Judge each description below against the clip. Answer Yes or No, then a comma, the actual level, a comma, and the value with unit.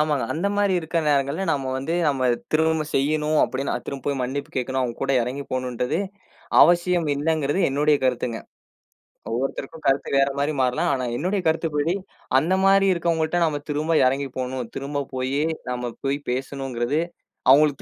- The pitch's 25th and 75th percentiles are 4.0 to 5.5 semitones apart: No, average, 3.3 semitones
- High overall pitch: No, medium, 140 Hz